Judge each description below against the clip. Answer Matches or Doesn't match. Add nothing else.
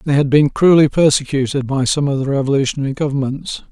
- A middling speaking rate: Matches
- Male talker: Matches